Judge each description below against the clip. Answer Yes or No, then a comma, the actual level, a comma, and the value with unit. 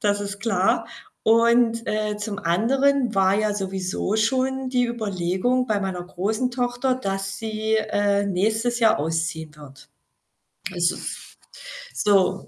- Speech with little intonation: No, average, 3.5 semitones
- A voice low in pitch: No, high, 210 Hz